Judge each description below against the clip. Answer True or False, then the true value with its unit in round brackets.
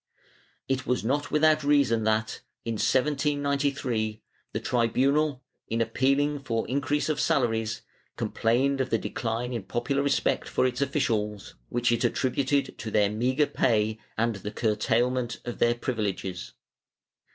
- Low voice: True (125 Hz)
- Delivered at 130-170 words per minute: True (140 wpm)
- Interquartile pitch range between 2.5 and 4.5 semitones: True (3.8 semitones)